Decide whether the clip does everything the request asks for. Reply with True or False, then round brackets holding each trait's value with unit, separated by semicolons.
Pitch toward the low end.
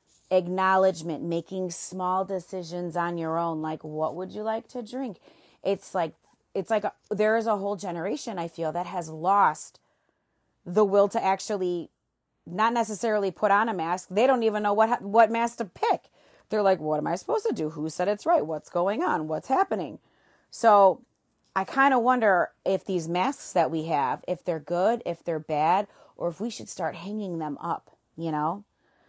False (190 Hz)